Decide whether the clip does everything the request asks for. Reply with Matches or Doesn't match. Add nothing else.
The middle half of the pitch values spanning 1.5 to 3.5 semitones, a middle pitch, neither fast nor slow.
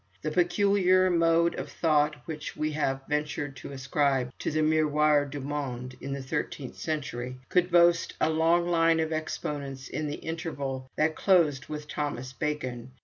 Matches